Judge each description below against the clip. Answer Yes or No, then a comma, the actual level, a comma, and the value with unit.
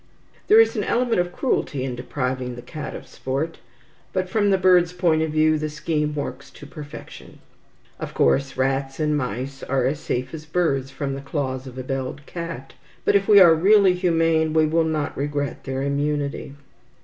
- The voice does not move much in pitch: No, average, 3.6 semitones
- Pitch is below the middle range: No, medium, 150 Hz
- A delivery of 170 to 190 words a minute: Yes, average, 185 wpm